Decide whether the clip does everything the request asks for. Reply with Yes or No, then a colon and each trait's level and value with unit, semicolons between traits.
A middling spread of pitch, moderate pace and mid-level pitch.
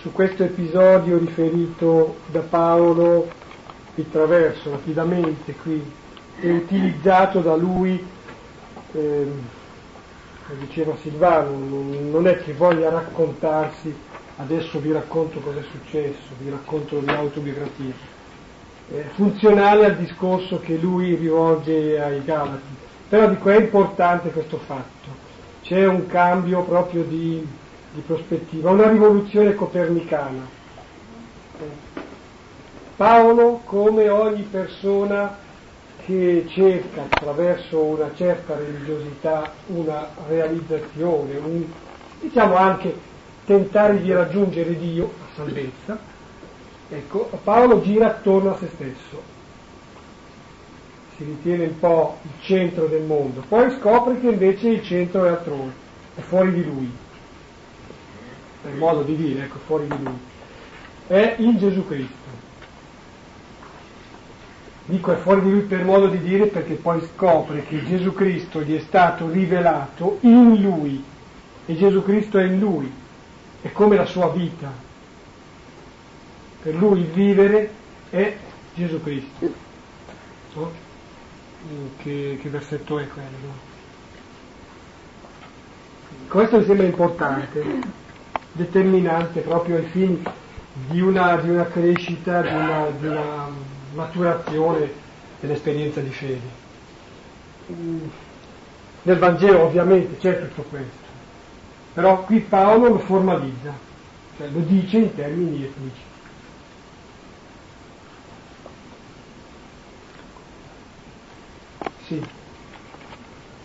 No: average, 4.2 semitones; slow, 105 wpm; medium, 165 Hz